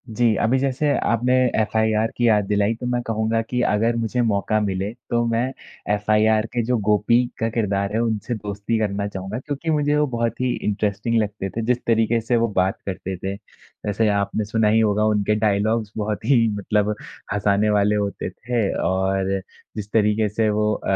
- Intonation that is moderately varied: No, narrow, 2.1 semitones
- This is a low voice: Yes, low, 110 Hz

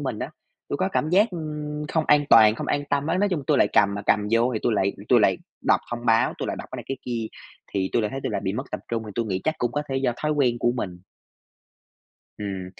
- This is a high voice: No, low, 120 Hz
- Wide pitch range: Yes, wide, 5.9 semitones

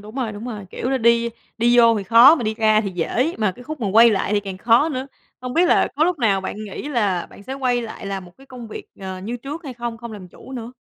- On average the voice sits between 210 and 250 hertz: Yes, high, 230 Hz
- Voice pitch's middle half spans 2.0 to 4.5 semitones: Yes, average, 3.5 semitones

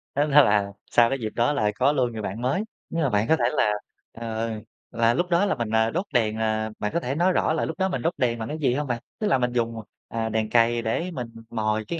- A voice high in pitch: No, low, 120 Hz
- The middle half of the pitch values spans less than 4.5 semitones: No, average, 4.8 semitones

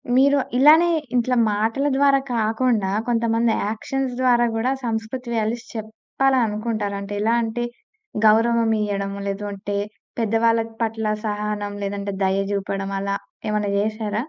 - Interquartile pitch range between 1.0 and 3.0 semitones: Yes, narrow, 2.4 semitones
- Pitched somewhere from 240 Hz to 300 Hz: No, high, 220 Hz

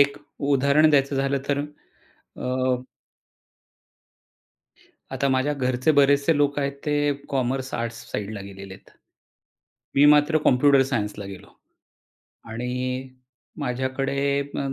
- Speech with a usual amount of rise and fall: No, narrow, 2.1 semitones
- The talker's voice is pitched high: No, low, 135 Hz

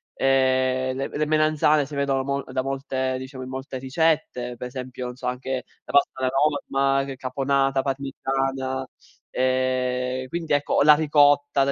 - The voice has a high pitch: No, low, 135 Hz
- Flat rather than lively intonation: Yes, narrow, 1.4 semitones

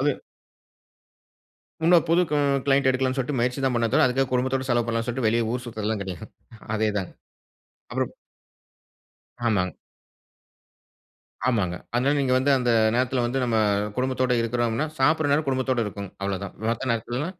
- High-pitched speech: No, low, 125 Hz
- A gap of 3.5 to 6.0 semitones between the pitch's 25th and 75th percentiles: No, narrow, 2.6 semitones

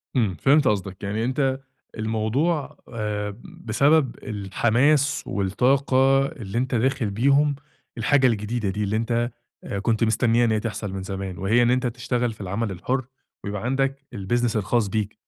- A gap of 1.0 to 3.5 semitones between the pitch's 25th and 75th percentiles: No, average, 4.0 semitones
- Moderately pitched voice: No, low, 115 Hz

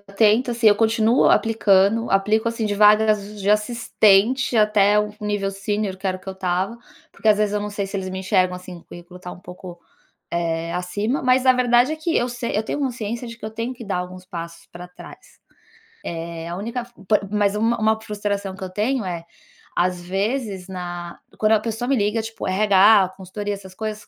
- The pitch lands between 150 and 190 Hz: No, high, 205 Hz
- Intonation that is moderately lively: Yes, average, 3.1 semitones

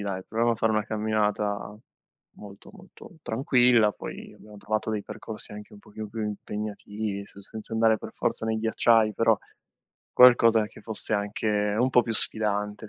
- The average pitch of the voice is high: No, low, 110 Hz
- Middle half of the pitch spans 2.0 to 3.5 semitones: No, narrow, 1.4 semitones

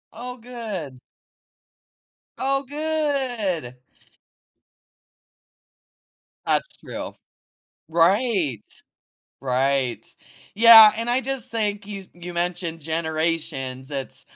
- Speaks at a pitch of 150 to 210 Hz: Yes, high, 190 Hz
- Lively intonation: Yes, wide, 7.3 semitones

